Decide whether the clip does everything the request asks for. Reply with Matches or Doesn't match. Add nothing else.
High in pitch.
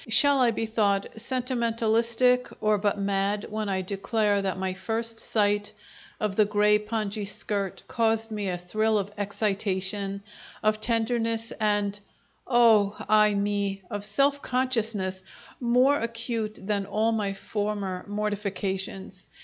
Matches